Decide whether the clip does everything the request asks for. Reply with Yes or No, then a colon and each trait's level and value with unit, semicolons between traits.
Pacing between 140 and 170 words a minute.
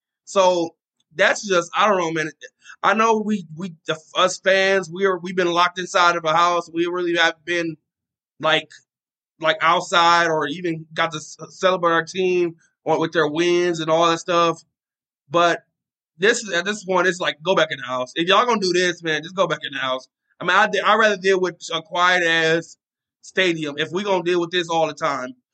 No: fast, 205 wpm